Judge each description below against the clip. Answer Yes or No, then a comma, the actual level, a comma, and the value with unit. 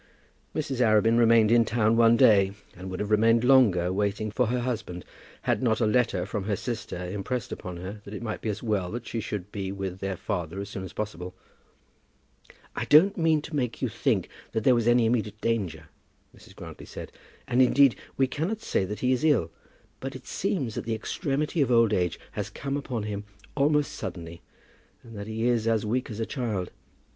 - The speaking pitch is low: Yes, low, 110 Hz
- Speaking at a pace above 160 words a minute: Yes, fast, 205 wpm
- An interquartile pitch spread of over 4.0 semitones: No, average, 3.7 semitones